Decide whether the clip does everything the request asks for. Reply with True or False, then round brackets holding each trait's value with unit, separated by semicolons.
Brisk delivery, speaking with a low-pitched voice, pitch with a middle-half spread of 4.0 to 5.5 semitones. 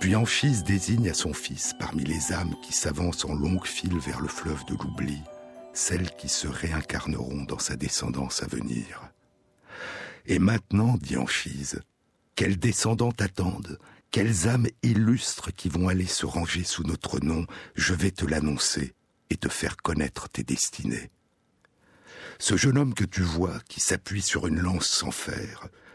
False (160 wpm; 90 Hz; 4.5 semitones)